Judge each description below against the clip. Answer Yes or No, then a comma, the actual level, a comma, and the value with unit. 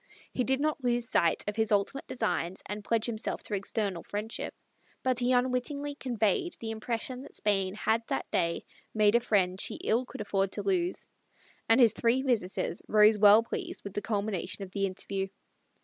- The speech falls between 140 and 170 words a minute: No, average, 180 wpm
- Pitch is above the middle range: Yes, high, 220 Hz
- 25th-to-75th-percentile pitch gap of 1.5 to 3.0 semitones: No, average, 3.8 semitones